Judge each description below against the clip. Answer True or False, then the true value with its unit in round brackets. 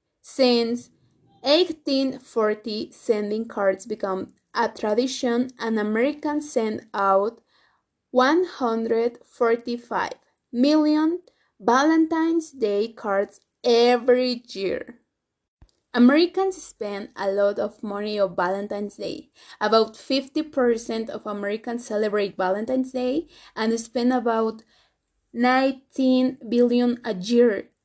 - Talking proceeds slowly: True (90 wpm)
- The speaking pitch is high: True (240 Hz)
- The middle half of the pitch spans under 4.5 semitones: True (3.7 semitones)